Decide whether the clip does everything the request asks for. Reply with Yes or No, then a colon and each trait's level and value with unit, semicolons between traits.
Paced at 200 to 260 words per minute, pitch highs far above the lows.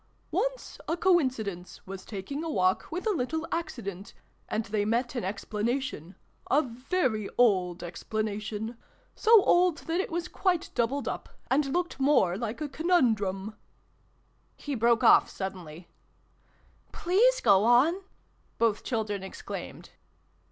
No: average, 145 wpm; wide, 7.9 semitones